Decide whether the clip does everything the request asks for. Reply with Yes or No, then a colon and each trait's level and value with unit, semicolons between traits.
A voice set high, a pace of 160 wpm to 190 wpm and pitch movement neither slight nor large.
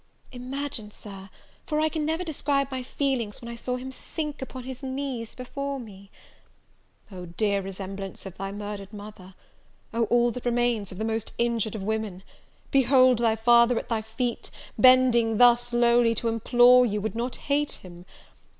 Yes: high, 235 Hz; average, 170 wpm; average, 3.5 semitones